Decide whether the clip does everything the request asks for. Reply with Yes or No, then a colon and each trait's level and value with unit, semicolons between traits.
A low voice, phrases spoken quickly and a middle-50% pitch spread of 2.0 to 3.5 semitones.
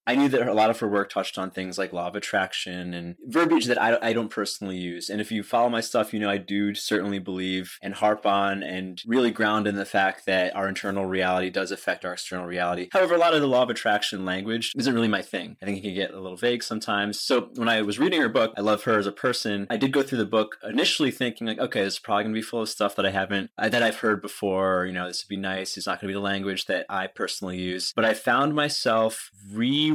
Yes: low, 100 Hz; fast, 270 wpm; average, 3.0 semitones